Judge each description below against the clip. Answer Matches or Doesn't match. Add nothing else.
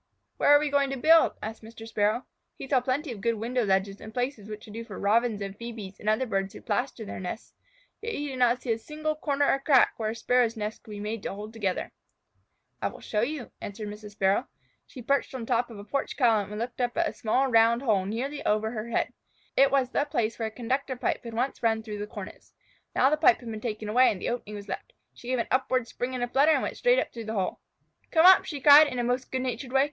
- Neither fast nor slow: Doesn't match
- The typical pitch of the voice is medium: Doesn't match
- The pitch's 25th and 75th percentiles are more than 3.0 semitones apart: Matches